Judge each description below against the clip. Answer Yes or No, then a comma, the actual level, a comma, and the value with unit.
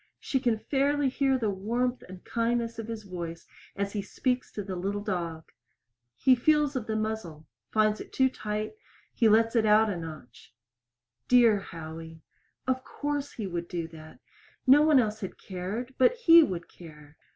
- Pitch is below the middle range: No, high, 215 Hz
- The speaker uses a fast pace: No, average, 175 wpm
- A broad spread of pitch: Yes, wide, 5.9 semitones